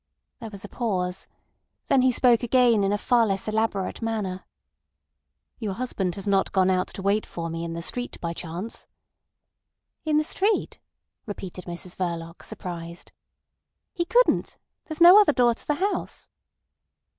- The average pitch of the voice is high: Yes, high, 205 Hz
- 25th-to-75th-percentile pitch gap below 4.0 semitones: No, average, 5.3 semitones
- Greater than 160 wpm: No, average, 155 wpm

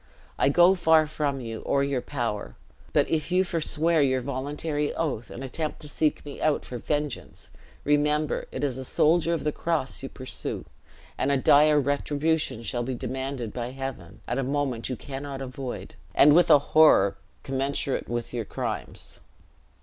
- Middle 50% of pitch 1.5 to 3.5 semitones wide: Yes, average, 2.9 semitones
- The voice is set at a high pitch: No, medium, 140 Hz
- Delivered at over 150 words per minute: Yes, average, 170 wpm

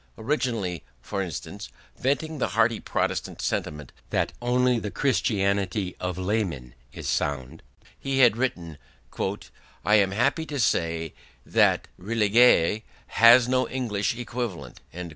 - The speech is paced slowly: Yes, slow, 120 wpm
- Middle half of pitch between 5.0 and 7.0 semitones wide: Yes, wide, 5.4 semitones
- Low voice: Yes, low, 105 Hz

